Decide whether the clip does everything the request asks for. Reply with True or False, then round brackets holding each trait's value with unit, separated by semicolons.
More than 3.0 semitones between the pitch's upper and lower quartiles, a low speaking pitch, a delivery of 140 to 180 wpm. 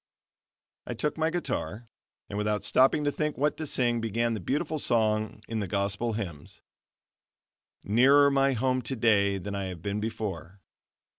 True (4.7 semitones; 115 Hz; 155 wpm)